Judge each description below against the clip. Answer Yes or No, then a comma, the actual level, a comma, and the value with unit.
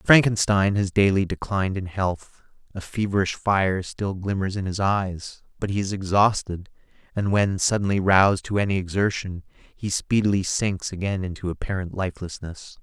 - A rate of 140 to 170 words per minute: Yes, average, 150 wpm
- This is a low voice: Yes, very low, 95 Hz